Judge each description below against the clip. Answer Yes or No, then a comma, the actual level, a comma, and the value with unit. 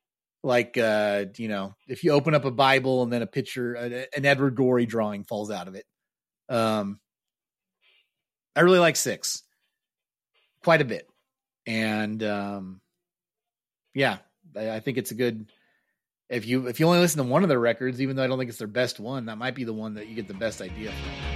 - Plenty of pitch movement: No, average, 3.8 semitones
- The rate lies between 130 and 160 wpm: No, average, 195 wpm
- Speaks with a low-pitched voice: Yes, low, 120 Hz